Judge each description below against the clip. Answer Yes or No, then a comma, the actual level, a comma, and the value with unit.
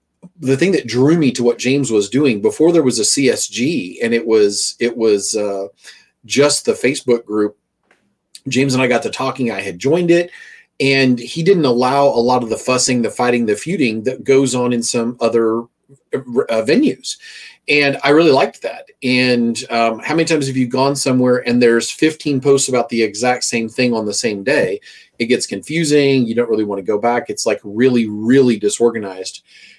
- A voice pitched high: No, low, 125 Hz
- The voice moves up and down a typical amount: Yes, average, 3.2 semitones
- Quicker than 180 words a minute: Yes, average, 195 wpm